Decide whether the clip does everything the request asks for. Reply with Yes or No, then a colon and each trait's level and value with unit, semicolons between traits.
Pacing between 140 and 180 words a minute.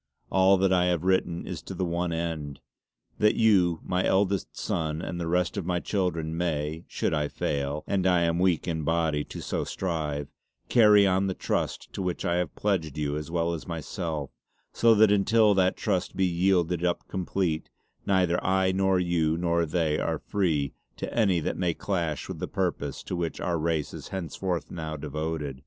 No: average, 190 wpm